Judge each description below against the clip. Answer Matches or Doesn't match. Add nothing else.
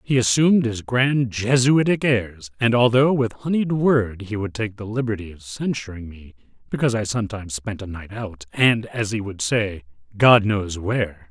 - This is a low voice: Matches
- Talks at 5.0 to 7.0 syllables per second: Doesn't match